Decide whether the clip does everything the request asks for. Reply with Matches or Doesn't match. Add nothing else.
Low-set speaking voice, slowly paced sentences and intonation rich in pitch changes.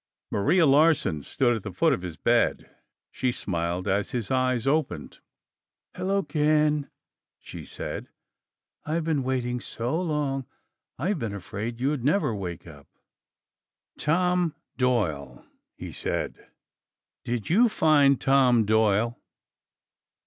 Matches